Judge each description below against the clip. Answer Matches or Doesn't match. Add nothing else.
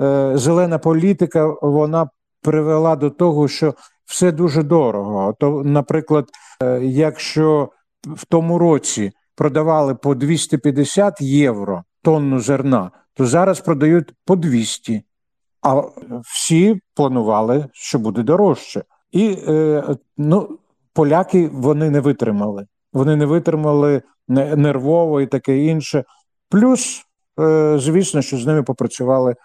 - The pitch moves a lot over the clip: Doesn't match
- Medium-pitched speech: Matches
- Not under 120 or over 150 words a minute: Doesn't match